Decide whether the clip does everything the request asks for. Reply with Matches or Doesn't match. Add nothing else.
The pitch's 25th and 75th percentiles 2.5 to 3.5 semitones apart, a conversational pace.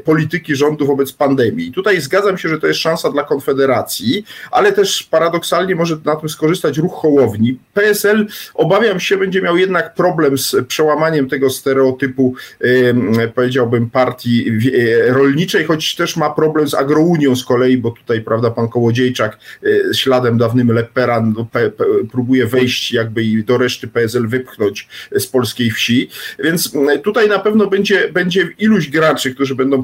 Doesn't match